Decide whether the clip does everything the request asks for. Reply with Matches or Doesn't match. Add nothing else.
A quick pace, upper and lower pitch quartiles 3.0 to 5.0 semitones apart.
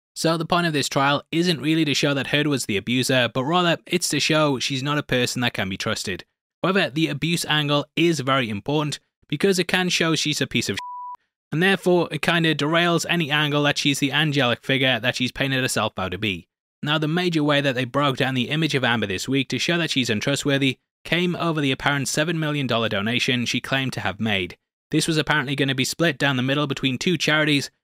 Matches